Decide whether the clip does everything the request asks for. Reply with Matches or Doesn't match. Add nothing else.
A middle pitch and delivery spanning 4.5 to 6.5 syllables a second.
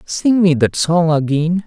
Doesn't match